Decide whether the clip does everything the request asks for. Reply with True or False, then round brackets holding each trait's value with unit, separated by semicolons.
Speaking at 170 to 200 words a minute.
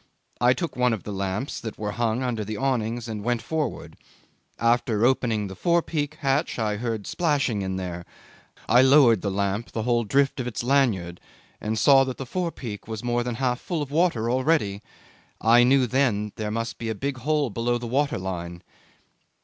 True (190 wpm)